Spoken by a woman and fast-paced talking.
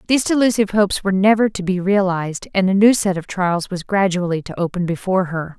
Yes: female; fast, 215 wpm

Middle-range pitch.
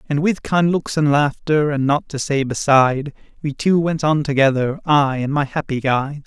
Yes: medium, 145 Hz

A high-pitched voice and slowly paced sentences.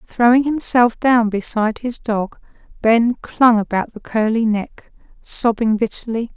Yes: high, 230 Hz; slow, 130 wpm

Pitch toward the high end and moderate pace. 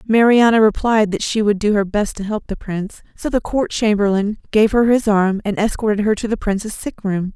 No: high, 210 Hz; fast, 230 wpm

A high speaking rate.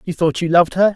Yes: fast, 315 wpm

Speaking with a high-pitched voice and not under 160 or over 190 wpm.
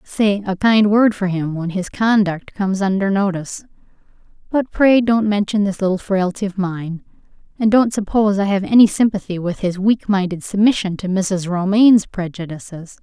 Yes: high, 195 Hz; average, 165 wpm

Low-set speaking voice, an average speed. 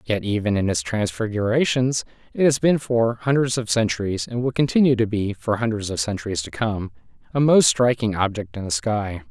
Yes: low, 110 Hz; average, 195 wpm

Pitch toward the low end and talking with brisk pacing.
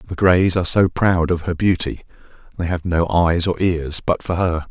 Yes: very low, 85 Hz; fast, 215 wpm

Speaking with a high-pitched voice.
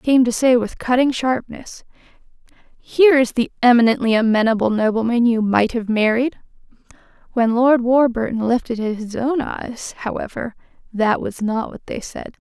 Yes: high, 240 Hz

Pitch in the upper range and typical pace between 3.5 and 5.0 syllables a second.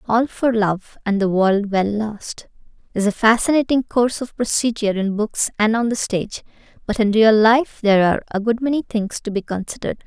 No: high, 220 Hz; 5.4 syllables/s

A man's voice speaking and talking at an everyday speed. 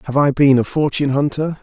No: male; fast, 220 wpm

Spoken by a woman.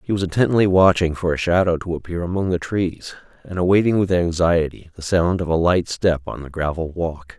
No: male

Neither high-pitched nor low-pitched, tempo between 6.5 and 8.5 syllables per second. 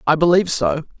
Yes: medium, 150 Hz; 6.8 syllables/s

